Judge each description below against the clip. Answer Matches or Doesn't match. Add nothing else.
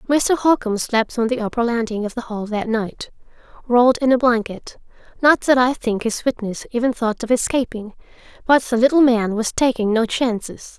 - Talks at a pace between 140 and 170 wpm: Doesn't match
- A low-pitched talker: Doesn't match